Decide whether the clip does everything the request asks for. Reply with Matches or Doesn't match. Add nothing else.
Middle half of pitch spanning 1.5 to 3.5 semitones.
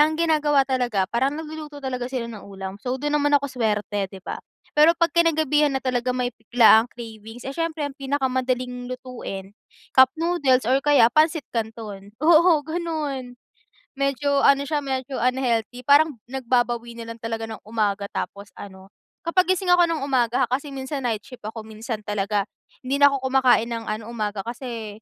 Doesn't match